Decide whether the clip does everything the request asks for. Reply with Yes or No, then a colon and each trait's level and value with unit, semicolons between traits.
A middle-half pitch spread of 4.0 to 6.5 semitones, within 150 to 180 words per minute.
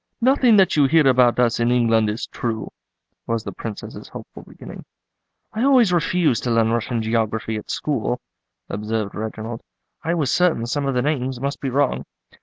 Yes: average, 5.0 semitones; average, 175 wpm